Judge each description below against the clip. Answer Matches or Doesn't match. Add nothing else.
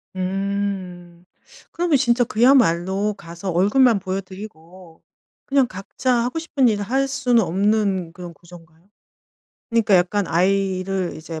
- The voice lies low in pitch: Doesn't match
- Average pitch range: Matches